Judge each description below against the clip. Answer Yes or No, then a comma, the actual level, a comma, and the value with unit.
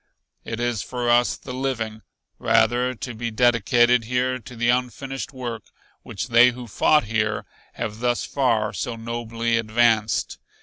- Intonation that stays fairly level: Yes, narrow, 1.7 semitones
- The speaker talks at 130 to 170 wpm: Yes, average, 145 wpm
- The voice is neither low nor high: No, low, 120 Hz